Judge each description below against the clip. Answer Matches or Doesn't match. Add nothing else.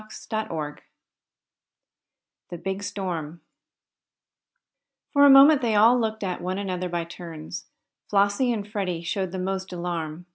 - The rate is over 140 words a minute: Doesn't match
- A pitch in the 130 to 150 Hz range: Doesn't match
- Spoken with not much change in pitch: Doesn't match